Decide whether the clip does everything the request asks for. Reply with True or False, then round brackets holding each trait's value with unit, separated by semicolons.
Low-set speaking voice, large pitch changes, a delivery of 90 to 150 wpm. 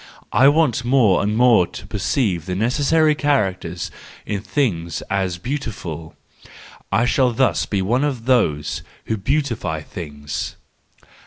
True (110 Hz; 6.9 semitones; 140 wpm)